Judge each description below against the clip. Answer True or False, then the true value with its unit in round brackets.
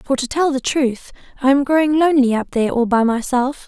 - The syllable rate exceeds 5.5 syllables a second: True (5.8 syllables/s)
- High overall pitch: True (265 Hz)